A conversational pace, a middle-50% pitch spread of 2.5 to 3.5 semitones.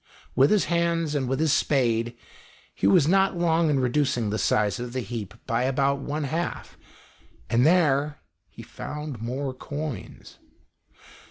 No: average, 150 wpm; average, 4.4 semitones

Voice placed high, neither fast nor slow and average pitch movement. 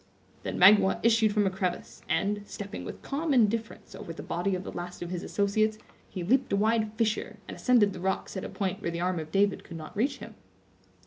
No: high, 200 Hz; fast, 220 wpm; average, 3.2 semitones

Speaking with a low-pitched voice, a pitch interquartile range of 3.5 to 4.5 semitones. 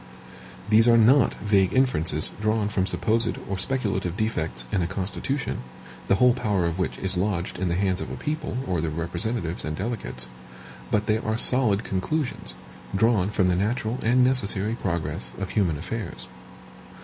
Yes: low, 100 Hz; average, 4.1 semitones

